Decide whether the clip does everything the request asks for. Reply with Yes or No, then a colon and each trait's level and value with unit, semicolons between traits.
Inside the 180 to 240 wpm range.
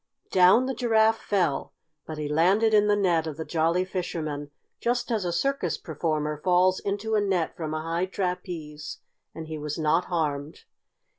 No: average, 170 wpm